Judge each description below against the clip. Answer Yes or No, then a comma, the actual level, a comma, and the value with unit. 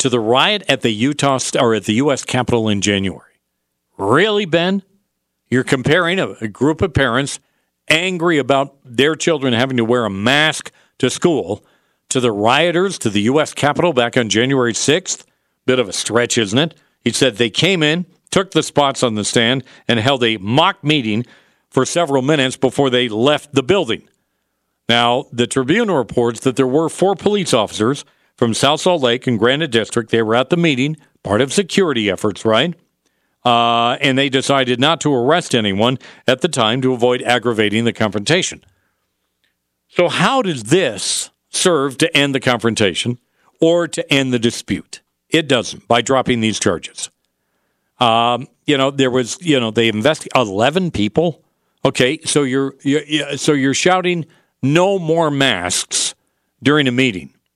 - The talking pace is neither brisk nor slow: Yes, average, 170 wpm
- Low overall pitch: Yes, low, 130 Hz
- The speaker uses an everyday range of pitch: Yes, average, 4.3 semitones